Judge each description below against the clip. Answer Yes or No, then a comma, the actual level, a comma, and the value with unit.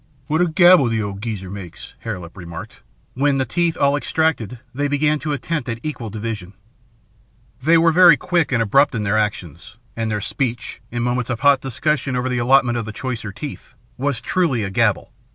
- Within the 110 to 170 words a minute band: No, average, 195 wpm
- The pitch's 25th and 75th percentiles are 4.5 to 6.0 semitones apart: Yes, average, 5.1 semitones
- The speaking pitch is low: Yes, low, 125 Hz